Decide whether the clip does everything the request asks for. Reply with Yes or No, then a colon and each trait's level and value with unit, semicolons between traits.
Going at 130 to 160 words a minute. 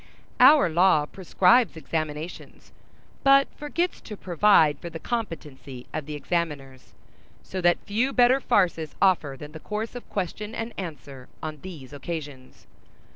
Yes: slow, 135 wpm